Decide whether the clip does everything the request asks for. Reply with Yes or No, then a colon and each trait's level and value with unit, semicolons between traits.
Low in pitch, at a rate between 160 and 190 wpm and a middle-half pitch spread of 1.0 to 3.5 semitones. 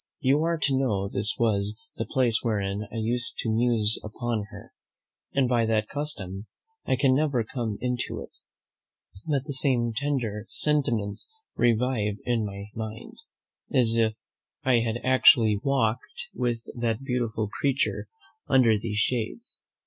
No: low, 115 Hz; average, 140 wpm; average, 3.1 semitones